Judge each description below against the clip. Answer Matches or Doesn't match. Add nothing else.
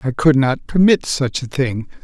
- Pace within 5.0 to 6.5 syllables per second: Doesn't match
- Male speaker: Matches